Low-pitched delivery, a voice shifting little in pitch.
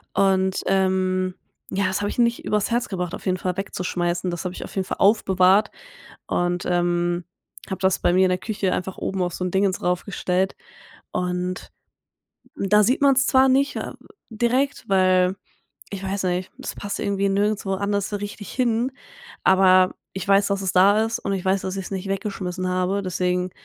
No: high, 190 Hz; narrow, 1.8 semitones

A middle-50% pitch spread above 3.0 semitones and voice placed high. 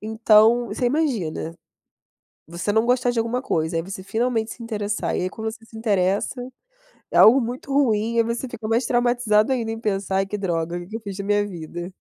Yes: average, 3.5 semitones; high, 220 Hz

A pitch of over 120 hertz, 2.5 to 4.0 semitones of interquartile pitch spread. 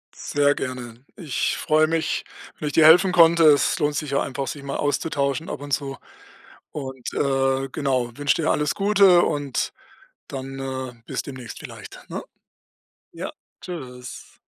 Yes: medium, 140 Hz; average, 2.8 semitones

